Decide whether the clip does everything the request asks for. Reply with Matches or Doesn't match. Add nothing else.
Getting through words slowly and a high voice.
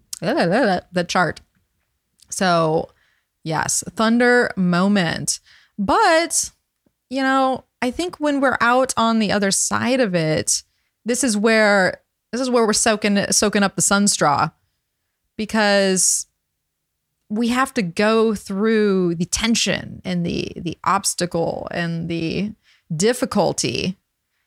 Matches